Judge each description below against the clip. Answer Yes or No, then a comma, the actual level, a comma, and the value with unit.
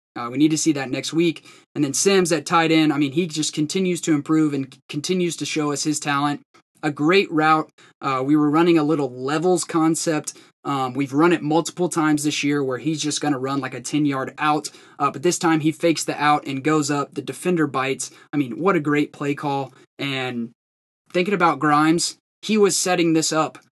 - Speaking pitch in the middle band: Yes, medium, 150 Hz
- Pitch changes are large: No, narrow, 2.5 semitones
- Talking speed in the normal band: No, fast, 225 wpm